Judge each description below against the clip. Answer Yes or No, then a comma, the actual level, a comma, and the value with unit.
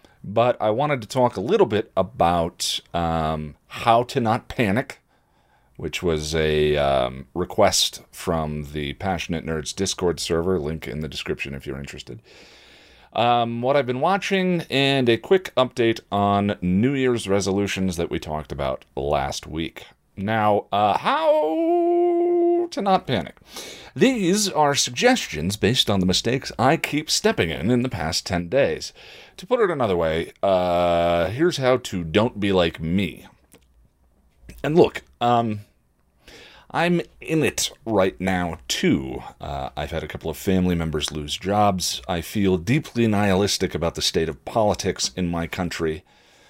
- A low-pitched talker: Yes, very low, 95 Hz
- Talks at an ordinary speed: Yes, average, 150 wpm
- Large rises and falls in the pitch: Yes, wide, 7.8 semitones